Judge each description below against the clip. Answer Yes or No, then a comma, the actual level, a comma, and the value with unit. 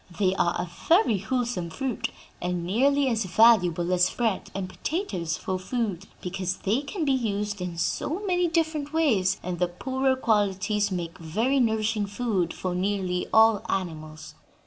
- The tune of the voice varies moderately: No, wide, 5.8 semitones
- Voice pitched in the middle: No, high, 205 Hz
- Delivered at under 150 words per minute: No, average, 155 wpm